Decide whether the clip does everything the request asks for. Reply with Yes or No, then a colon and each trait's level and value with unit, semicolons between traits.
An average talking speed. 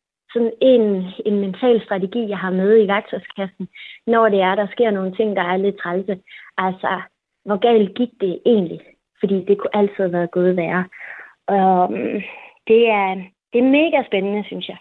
Yes: average, 180 wpm